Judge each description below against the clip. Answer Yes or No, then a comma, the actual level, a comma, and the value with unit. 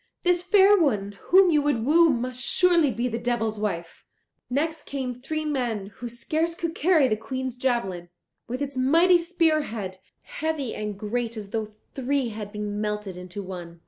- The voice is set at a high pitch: Yes, very high, 250 Hz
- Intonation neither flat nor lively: No, wide, 6.6 semitones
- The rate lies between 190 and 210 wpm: No, average, 175 wpm